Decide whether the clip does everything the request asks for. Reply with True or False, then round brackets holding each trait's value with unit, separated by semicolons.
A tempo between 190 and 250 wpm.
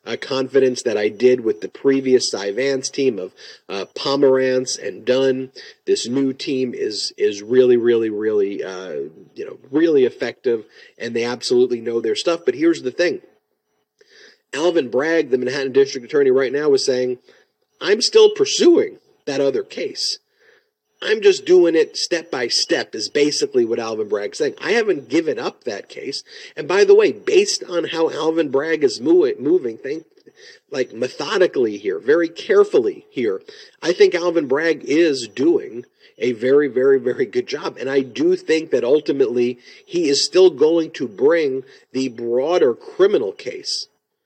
False (165 wpm)